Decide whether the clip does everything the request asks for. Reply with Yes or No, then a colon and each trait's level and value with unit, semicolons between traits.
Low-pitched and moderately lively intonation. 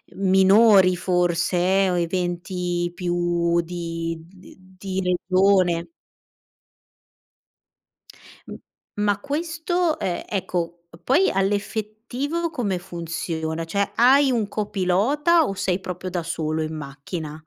No: medium, 185 Hz; average, 3.2 semitones